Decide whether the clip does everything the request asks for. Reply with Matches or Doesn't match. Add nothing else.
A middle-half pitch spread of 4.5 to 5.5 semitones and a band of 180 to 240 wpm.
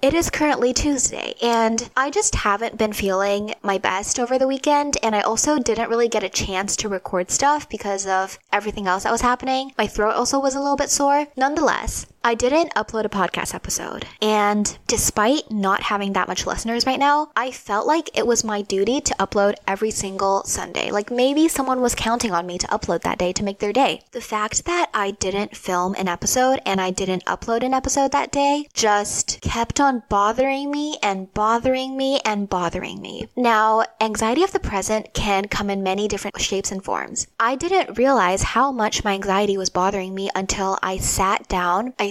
Matches